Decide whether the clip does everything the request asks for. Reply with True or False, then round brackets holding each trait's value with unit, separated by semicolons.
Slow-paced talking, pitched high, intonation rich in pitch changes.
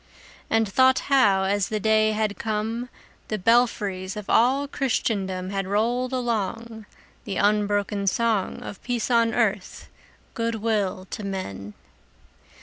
False (130 wpm; 215 Hz; 2.8 semitones)